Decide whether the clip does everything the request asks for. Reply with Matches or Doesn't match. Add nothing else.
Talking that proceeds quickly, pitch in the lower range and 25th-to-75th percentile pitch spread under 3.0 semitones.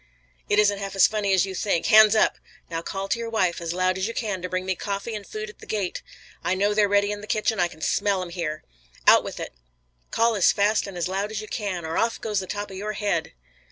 Doesn't match